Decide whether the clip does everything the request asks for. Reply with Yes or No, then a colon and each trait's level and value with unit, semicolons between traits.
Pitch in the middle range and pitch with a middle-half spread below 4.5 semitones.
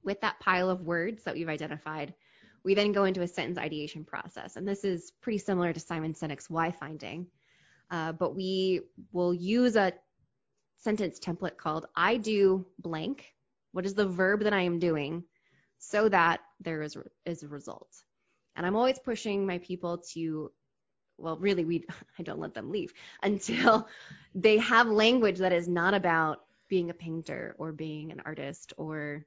Yes: medium, 180 Hz; average, 3.6 semitones